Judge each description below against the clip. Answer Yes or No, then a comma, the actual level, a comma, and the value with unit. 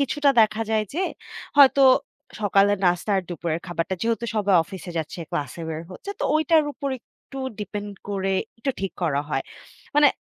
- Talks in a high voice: Yes, high, 205 Hz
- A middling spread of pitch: No, wide, 7.4 semitones